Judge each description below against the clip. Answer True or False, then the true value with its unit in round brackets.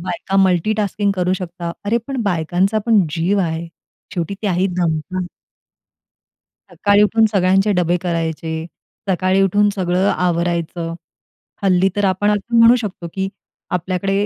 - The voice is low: False (185 Hz)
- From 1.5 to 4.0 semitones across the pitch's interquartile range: True (2.7 semitones)